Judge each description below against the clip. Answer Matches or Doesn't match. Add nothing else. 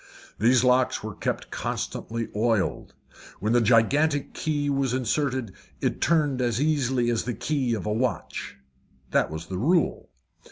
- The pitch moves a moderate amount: Matches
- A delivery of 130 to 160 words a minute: Matches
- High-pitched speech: Doesn't match